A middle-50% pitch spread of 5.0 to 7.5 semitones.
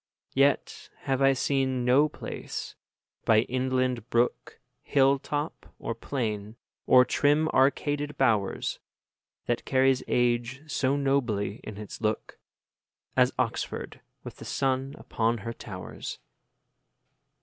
No: average, 3.0 semitones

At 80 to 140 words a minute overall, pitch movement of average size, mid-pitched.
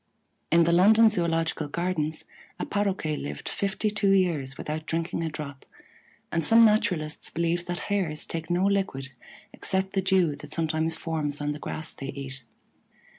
No: average, 160 wpm; average, 3.8 semitones; medium, 165 Hz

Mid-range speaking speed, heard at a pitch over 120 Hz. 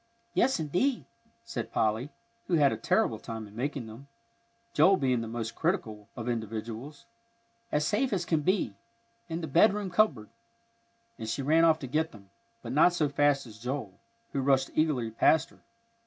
Yes: average, 170 wpm; low, 135 Hz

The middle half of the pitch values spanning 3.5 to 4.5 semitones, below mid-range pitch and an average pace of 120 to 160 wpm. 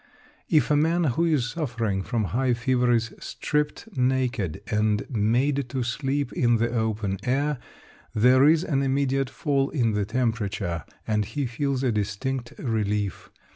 Yes: average, 3.9 semitones; low, 125 Hz; average, 150 wpm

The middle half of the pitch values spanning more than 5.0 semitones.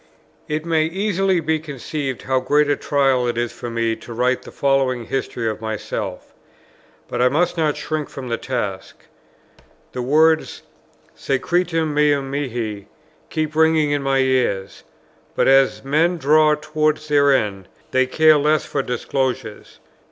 No: average, 3.8 semitones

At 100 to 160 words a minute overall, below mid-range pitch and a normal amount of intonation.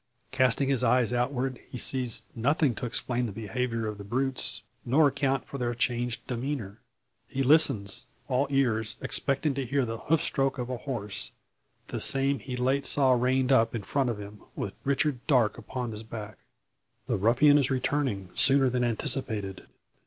No: average, 170 wpm; low, 125 Hz; average, 3.1 semitones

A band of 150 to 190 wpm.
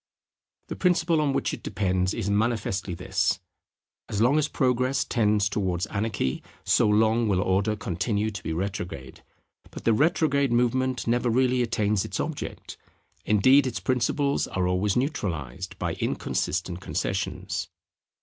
No: average, 140 wpm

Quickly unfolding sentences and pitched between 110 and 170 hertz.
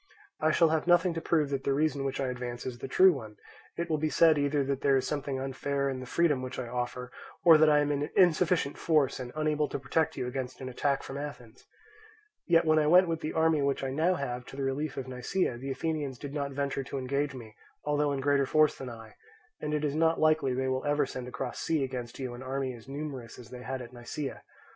Yes: fast, 245 wpm; medium, 140 Hz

